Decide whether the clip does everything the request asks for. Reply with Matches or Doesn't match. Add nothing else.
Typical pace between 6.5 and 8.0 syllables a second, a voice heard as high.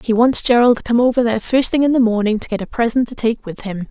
Matches